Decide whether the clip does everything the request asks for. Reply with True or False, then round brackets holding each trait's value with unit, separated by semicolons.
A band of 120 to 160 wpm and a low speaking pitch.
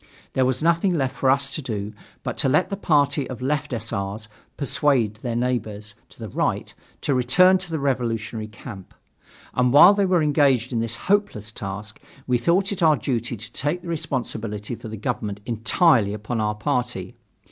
False (185 wpm; 125 Hz)